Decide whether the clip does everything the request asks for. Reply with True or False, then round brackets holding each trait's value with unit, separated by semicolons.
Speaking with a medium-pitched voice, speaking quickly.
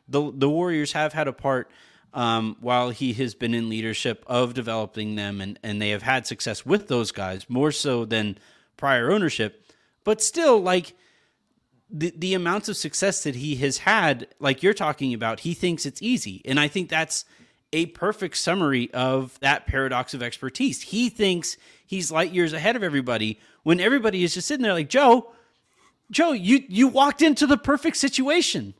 False (150 Hz; 180 wpm)